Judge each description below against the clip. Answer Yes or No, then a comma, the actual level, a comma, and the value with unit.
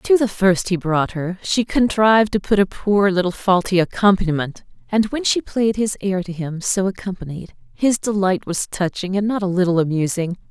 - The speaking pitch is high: Yes, high, 195 Hz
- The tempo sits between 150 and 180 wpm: No, average, 195 wpm